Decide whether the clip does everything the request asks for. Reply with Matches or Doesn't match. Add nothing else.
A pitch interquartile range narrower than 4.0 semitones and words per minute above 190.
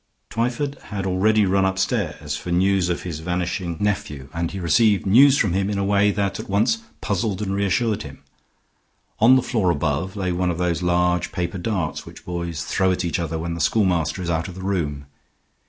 Matches